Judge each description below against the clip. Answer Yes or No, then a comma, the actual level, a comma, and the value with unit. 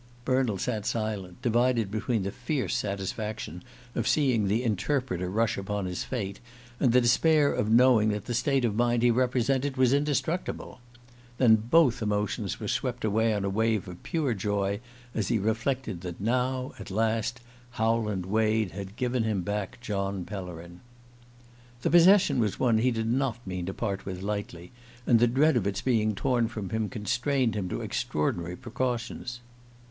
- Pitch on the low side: Yes, low, 110 Hz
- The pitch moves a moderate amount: Yes, average, 3.8 semitones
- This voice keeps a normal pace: Yes, average, 165 wpm